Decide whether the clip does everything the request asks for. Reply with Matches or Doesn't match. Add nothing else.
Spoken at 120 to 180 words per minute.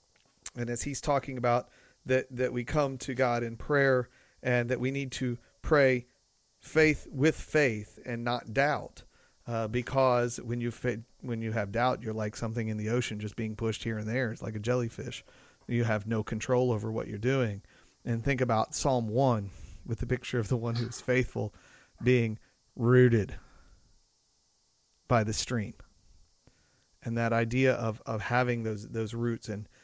Matches